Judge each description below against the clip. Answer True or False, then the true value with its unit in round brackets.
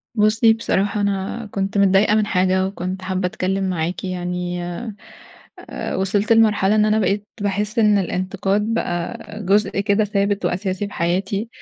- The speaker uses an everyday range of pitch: False (2.0 semitones)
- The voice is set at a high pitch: True (195 Hz)